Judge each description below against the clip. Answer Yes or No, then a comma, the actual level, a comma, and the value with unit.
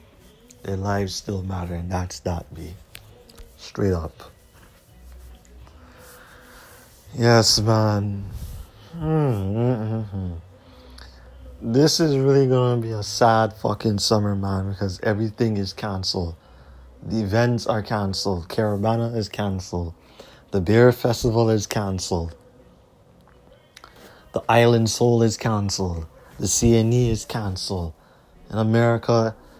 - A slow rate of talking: Yes, slow, 100 wpm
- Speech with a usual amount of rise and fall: Yes, average, 4.6 semitones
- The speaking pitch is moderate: No, low, 100 Hz